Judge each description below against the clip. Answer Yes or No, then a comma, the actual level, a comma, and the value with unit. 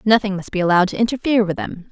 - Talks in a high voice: Yes, high, 200 Hz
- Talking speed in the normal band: No, fast, 250 wpm